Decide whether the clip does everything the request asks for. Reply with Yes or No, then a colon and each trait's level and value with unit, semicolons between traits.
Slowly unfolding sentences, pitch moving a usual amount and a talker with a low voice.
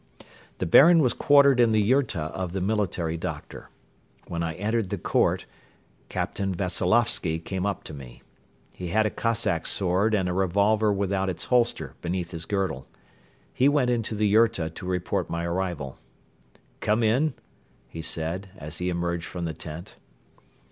No: average, 160 wpm; average, 4.4 semitones; very low, 95 Hz